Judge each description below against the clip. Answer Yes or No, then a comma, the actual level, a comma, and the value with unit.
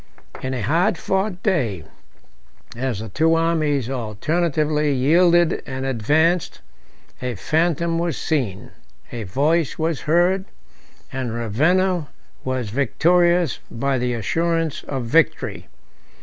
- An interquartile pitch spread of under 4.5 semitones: No, average, 5.2 semitones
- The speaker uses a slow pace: Yes, slow, 110 wpm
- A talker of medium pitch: Yes, medium, 150 Hz